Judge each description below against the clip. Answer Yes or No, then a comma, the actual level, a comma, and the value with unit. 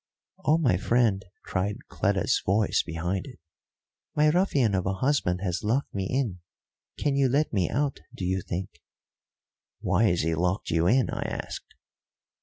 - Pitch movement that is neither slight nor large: No, wide, 6.5 semitones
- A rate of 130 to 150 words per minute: No, average, 160 wpm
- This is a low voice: Yes, low, 100 Hz